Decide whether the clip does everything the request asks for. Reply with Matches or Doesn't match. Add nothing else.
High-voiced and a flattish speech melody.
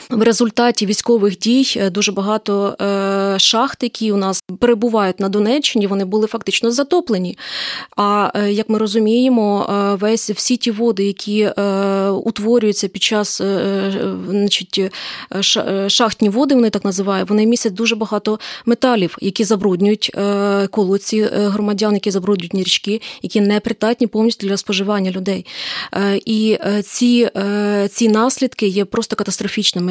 Matches